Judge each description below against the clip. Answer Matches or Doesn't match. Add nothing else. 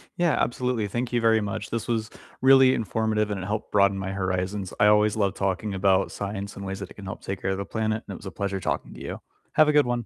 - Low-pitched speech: Matches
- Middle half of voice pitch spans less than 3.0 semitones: Matches